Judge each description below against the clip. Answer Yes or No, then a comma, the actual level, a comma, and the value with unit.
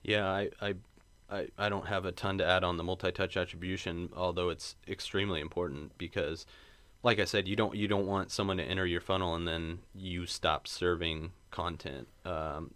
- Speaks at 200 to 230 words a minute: No, average, 190 wpm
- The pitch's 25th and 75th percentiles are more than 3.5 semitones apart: No, average, 2.7 semitones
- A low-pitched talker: Yes, very low, 90 Hz